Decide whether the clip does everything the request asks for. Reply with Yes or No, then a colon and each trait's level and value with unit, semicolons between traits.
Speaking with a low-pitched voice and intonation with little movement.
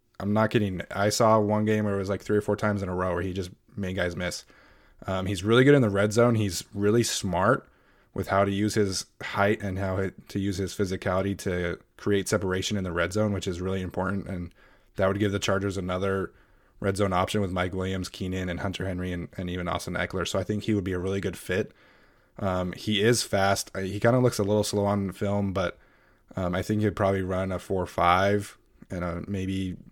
Yes: very low, 95 Hz; narrow, 1.9 semitones